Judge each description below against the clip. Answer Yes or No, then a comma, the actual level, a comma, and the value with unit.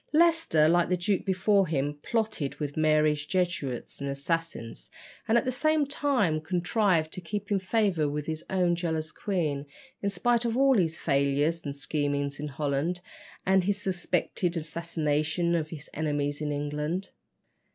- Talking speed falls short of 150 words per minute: No, average, 155 wpm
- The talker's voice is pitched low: No, medium, 165 Hz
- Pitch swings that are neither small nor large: Yes, average, 4.5 semitones